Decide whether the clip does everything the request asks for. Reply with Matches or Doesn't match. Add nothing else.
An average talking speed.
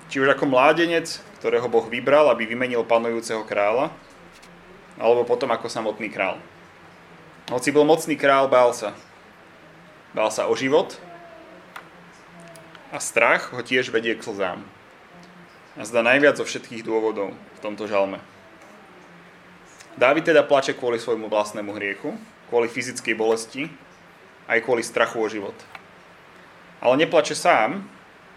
Matches